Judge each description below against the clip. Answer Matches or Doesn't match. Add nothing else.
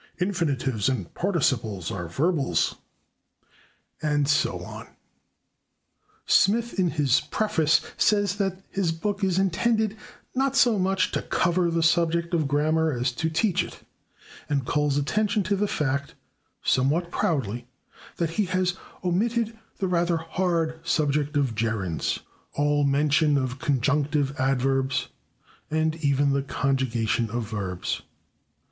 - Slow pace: Matches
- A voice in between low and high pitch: Matches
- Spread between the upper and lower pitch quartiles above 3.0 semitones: Matches